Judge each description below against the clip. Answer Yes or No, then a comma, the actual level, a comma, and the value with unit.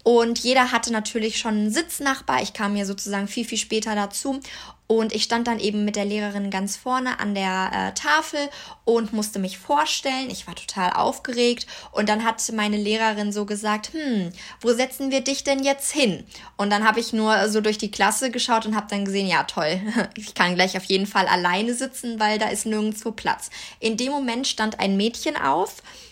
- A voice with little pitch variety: No, average, 3.2 semitones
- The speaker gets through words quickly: Yes, fast, 200 wpm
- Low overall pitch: No, high, 220 Hz